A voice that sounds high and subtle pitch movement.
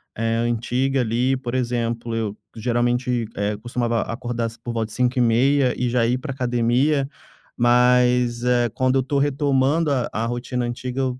No: low, 120 Hz; narrow, 1.7 semitones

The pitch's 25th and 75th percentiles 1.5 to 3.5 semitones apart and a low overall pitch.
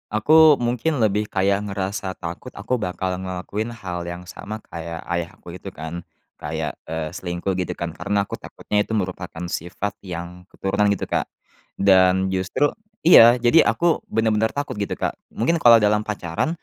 No: average, 4.0 semitones; low, 100 Hz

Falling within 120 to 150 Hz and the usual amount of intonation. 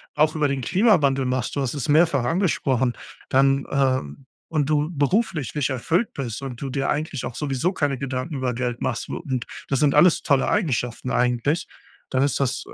Yes: medium, 140 Hz; average, 3.0 semitones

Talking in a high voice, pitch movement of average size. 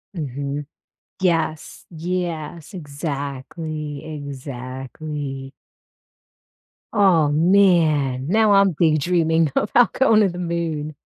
No: medium, 155 Hz; average, 3.6 semitones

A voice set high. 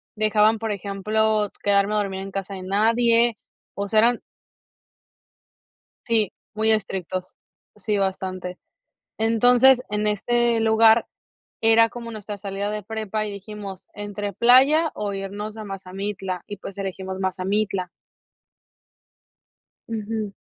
Yes: high, 210 Hz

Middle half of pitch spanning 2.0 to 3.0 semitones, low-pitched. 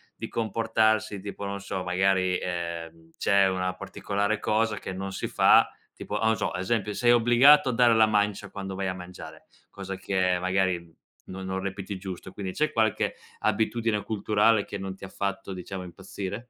Yes: narrow, 2.6 semitones; low, 100 Hz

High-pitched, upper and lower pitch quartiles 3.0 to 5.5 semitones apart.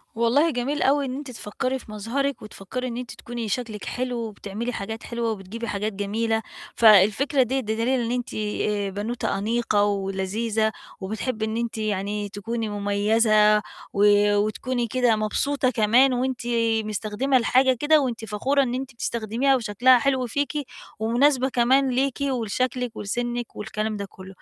Yes: high, 230 Hz; average, 3.3 semitones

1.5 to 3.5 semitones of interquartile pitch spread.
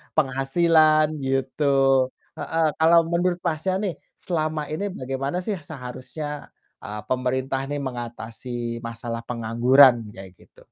No: average, 4.2 semitones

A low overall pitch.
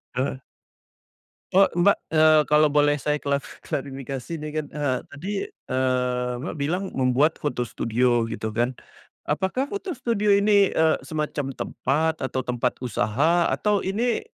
No: medium, 145 Hz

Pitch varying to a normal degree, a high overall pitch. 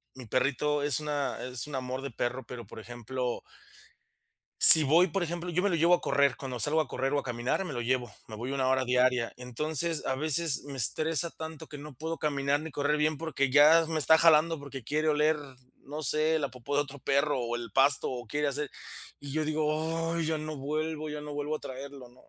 No: average, 3.1 semitones; medium, 145 Hz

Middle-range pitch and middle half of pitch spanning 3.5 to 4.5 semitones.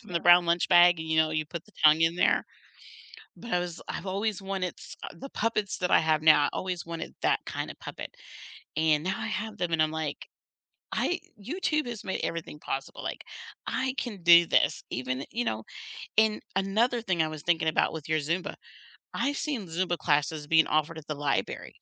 Yes: medium, 170 Hz; average, 4.0 semitones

